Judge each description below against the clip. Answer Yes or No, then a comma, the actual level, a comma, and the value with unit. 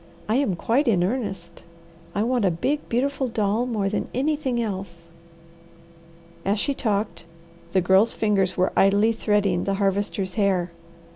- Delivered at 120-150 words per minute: Yes, average, 145 wpm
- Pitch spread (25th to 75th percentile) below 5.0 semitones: Yes, average, 3.7 semitones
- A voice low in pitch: No, high, 205 Hz